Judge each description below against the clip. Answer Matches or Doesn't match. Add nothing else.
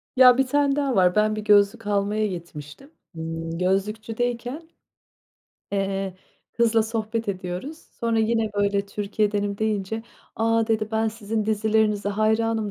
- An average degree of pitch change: Doesn't match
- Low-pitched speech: Doesn't match